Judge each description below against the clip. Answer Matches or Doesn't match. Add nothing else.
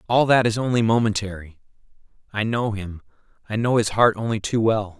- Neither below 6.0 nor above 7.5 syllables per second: Doesn't match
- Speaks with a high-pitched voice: Doesn't match